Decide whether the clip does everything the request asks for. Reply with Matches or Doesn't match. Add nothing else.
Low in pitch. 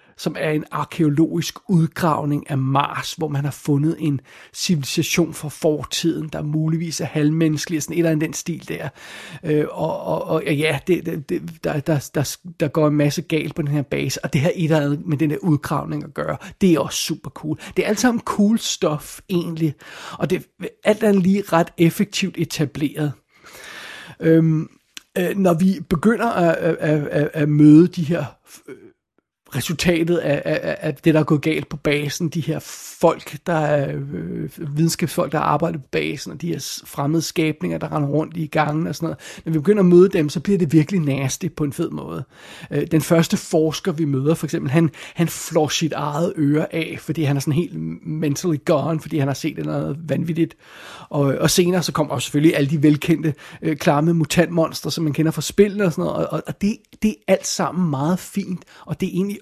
Doesn't match